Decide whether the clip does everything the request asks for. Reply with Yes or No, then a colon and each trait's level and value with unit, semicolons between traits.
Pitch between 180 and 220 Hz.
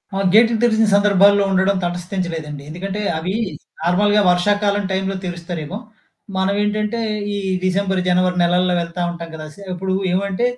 Yes: high, 190 Hz